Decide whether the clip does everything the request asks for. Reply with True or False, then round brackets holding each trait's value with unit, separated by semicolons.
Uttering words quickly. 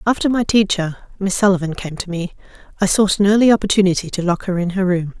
True (220 wpm)